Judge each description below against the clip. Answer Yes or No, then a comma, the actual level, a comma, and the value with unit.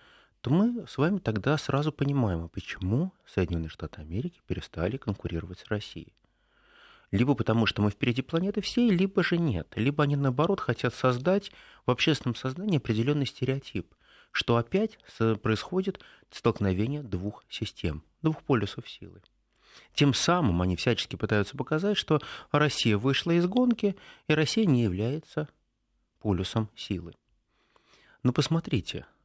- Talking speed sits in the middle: Yes, average, 130 wpm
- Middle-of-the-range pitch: No, low, 130 Hz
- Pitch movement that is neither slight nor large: No, wide, 6.8 semitones